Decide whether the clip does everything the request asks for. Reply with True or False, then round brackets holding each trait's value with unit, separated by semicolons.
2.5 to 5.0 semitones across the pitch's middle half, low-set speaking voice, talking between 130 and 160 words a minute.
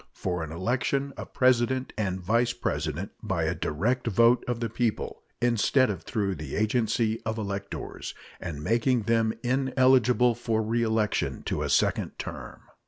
True (3.3 semitones; 115 Hz; 150 wpm)